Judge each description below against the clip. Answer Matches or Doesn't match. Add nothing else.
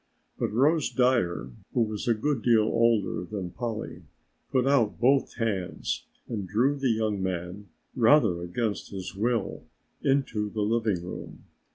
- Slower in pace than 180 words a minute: Matches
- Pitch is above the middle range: Doesn't match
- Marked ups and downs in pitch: Doesn't match